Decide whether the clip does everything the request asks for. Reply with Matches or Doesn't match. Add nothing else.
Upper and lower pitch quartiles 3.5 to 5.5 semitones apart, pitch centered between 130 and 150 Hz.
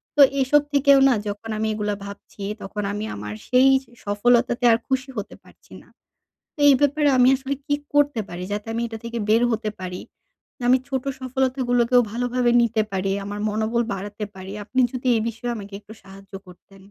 Doesn't match